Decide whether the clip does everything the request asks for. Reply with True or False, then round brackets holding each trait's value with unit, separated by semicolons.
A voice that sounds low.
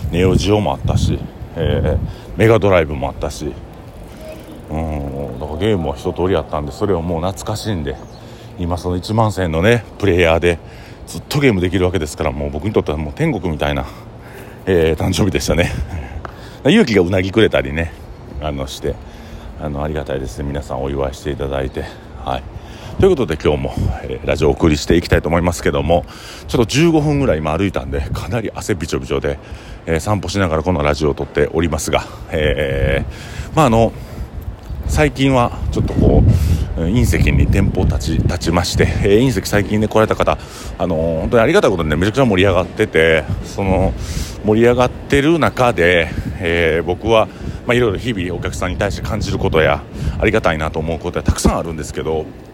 True (90 Hz)